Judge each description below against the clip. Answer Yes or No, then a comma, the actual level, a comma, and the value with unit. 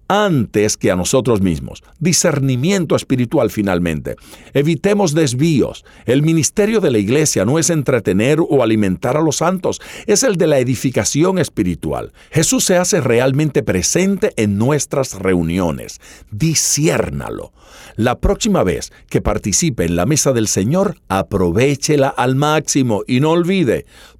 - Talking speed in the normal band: Yes, average, 135 wpm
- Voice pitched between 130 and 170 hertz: Yes, medium, 140 Hz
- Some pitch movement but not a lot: No, wide, 7.6 semitones